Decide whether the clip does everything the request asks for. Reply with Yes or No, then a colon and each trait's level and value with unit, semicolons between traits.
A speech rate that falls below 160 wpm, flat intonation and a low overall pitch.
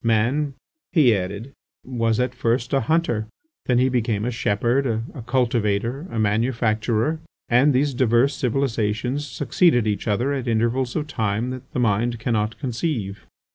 No: average, 145 wpm; average, 3.1 semitones; low, 120 Hz